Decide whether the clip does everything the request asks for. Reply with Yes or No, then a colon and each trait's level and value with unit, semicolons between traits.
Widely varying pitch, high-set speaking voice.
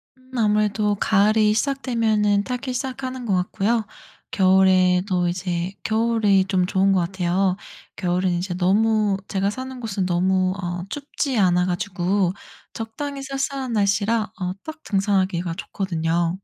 No: average, 3.6 semitones; high, 200 Hz